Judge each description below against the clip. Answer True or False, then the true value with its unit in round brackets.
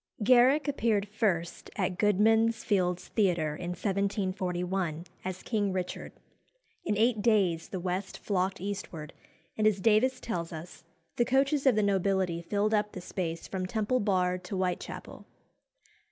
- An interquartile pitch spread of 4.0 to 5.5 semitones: False (3.2 semitones)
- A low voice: False (195 Hz)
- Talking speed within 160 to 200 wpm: False (140 wpm)